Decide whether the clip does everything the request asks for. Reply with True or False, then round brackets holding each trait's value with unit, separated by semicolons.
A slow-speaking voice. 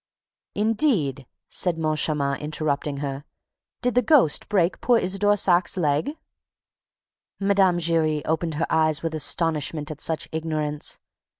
True (120 wpm)